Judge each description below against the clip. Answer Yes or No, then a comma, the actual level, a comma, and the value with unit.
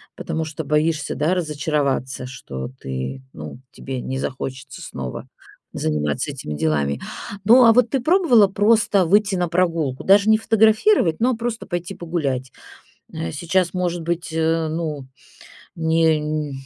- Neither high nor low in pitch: Yes, medium, 160 Hz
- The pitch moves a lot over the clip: Yes, wide, 6.7 semitones